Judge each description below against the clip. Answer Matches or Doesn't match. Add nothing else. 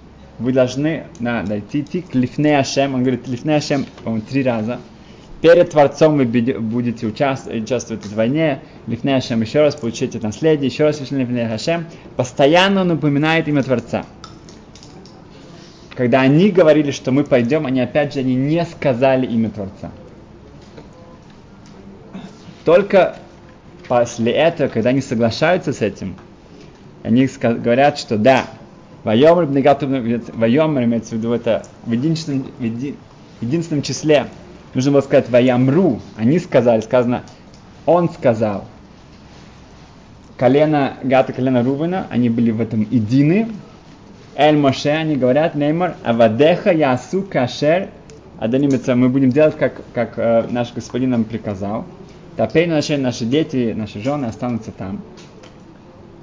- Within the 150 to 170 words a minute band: Doesn't match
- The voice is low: Matches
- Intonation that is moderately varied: Matches